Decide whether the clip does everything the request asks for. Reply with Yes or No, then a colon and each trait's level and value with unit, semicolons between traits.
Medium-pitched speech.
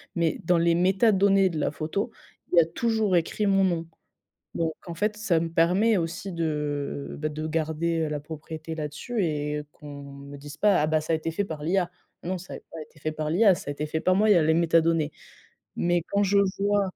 Yes: medium, 165 Hz